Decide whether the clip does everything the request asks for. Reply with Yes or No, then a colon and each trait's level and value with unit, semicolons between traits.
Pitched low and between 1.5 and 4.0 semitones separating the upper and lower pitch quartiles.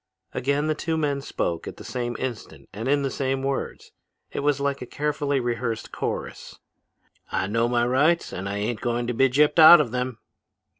Yes: low, 130 Hz; average, 3.2 semitones